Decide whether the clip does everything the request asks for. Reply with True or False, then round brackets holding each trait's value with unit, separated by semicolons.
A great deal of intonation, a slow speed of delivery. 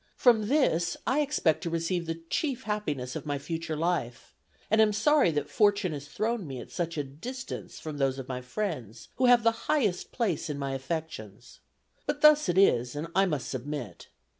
False (7.4 semitones; 190 wpm)